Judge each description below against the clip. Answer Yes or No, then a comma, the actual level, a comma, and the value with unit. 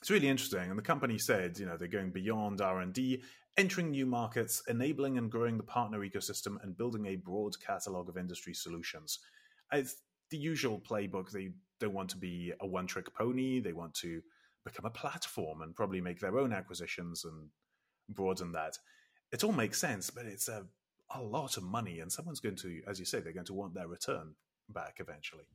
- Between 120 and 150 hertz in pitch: No, low, 100 Hz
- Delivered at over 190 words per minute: Yes, average, 200 wpm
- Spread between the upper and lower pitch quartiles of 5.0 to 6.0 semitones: Yes, wide, 5.6 semitones